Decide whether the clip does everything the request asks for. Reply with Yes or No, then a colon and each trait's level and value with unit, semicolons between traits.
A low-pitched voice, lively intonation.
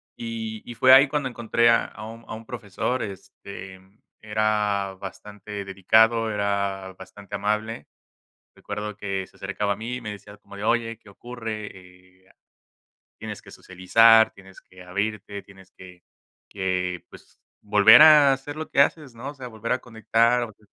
No: low, 105 Hz; average, 2.9 semitones